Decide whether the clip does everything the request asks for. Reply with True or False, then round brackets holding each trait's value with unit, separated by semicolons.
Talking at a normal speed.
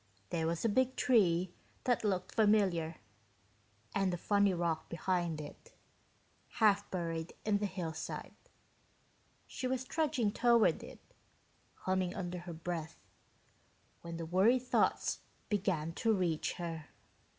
False (125 wpm)